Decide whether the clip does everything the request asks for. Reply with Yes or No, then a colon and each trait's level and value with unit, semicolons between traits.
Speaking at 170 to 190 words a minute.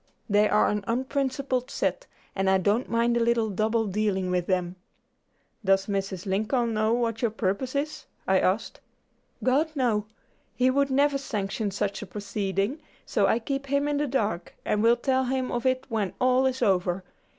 Yes: average, 175 wpm